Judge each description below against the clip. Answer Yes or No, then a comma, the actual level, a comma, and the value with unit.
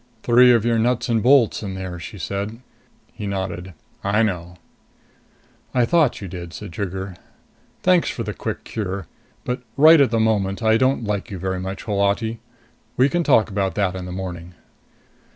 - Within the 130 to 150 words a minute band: No, average, 175 wpm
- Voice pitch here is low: Yes, low, 100 Hz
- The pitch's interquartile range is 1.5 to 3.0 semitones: No, average, 3.8 semitones